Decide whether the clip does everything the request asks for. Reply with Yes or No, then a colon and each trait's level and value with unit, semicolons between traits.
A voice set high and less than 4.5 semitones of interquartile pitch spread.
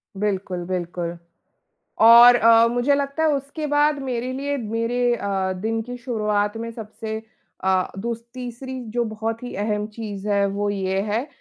Yes: high, 225 Hz; average, 3.3 semitones